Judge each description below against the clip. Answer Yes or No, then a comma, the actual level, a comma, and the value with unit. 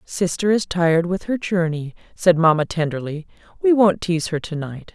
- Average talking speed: Yes, average, 180 wpm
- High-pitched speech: No, medium, 175 Hz